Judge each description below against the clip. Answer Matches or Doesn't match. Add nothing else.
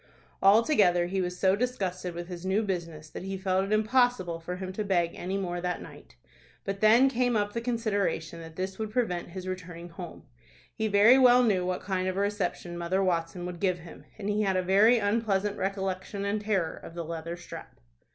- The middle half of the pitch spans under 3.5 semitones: Matches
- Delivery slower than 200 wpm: Doesn't match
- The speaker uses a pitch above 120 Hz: Matches